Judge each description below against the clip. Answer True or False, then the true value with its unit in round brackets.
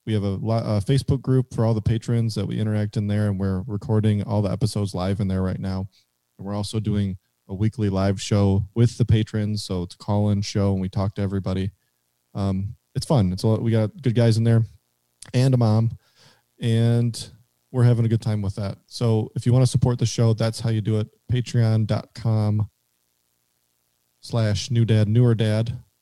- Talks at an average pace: False (210 wpm)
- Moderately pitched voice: False (110 Hz)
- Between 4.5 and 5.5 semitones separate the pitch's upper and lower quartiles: False (2.9 semitones)